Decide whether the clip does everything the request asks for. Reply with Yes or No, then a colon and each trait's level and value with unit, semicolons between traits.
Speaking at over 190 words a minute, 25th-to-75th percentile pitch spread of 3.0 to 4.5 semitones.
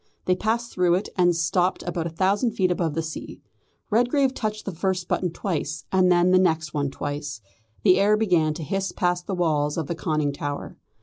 Yes: average, 200 wpm; average, 3.4 semitones